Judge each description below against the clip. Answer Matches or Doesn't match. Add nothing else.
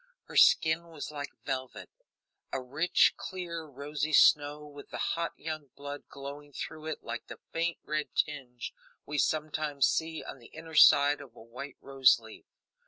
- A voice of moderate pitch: Matches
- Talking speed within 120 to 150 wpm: Doesn't match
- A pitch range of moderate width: Doesn't match